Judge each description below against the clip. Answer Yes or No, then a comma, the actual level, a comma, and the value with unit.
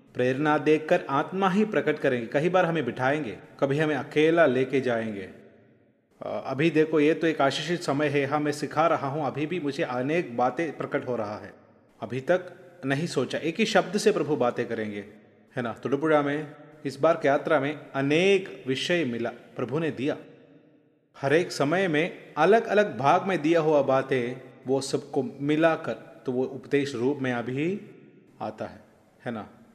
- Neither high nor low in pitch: Yes, medium, 145 Hz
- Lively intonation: No, average, 3.9 semitones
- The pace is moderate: No, fast, 175 wpm